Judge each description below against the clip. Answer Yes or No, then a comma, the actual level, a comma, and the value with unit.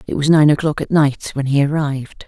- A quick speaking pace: Yes, fast, 235 wpm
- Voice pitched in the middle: Yes, medium, 145 Hz